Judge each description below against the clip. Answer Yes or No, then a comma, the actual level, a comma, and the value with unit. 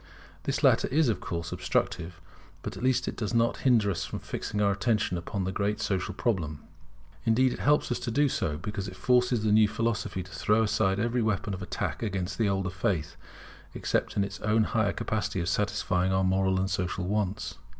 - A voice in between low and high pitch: No, low, 100 Hz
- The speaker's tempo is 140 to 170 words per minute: No, average, 200 wpm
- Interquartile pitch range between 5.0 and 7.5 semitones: No, average, 3.1 semitones